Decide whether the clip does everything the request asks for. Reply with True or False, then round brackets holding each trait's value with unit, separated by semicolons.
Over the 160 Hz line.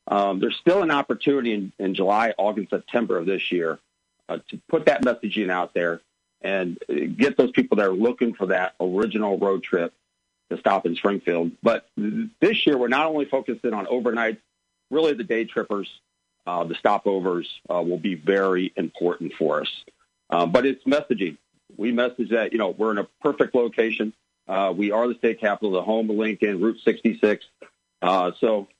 False (110 Hz)